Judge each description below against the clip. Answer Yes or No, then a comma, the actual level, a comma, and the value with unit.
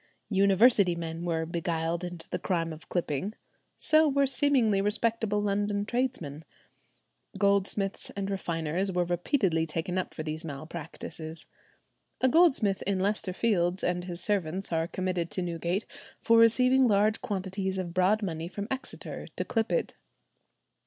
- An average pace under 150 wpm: Yes, average, 140 wpm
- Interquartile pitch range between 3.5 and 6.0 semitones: Yes, average, 3.8 semitones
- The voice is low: No, high, 190 Hz